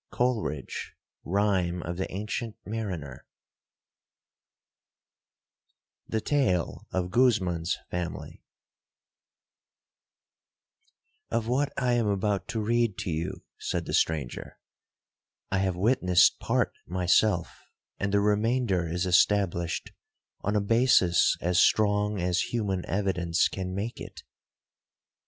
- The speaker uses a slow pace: Yes, slow, 100 wpm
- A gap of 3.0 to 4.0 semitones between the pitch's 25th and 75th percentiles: Yes, average, 3.5 semitones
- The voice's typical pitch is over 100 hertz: No, very low, 95 Hz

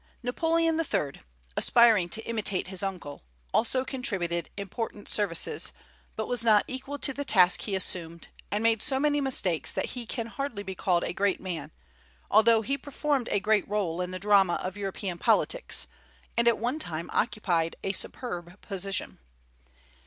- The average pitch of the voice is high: Yes, high, 205 Hz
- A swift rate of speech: No, average, 160 wpm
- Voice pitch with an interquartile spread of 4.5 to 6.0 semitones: Yes, average, 5.1 semitones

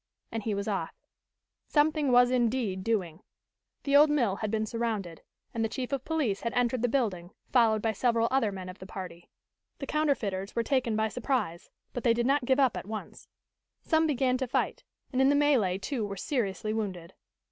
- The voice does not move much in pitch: No, average, 4.7 semitones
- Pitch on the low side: No, high, 230 Hz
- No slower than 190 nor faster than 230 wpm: Yes, average, 195 wpm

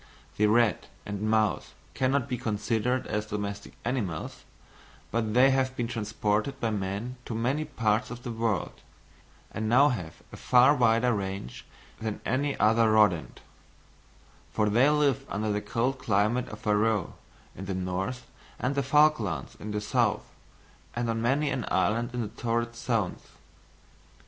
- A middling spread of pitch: Yes, average, 3.1 semitones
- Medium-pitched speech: No, low, 115 Hz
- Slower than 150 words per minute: No, average, 155 wpm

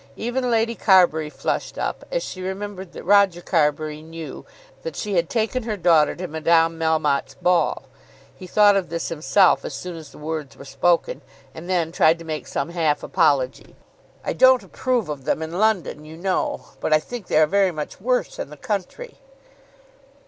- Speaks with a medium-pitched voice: Yes, medium, 170 Hz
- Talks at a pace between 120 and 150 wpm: No, average, 185 wpm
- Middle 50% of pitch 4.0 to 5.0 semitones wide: Yes, average, 4.5 semitones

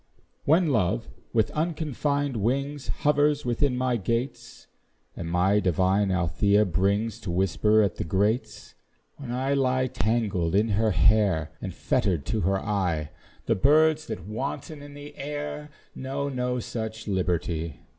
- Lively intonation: Yes, wide, 6.4 semitones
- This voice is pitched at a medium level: No, low, 110 Hz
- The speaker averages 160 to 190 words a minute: No, average, 140 wpm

